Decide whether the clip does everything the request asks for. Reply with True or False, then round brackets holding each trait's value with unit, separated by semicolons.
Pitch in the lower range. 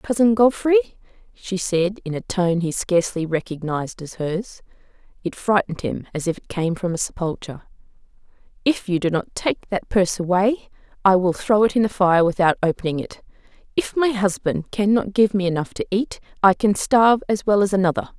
False (190 Hz)